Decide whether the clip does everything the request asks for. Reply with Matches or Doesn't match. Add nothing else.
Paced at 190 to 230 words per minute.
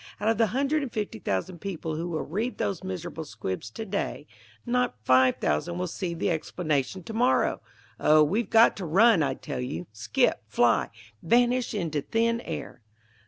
Doesn't match